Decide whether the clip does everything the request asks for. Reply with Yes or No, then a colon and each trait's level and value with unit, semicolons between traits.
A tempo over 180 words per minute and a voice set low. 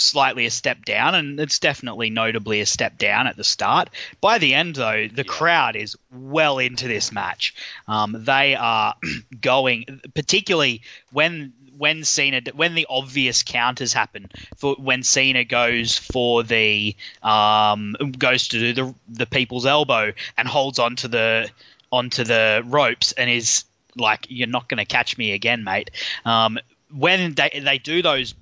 No: average, 160 wpm; low, 125 Hz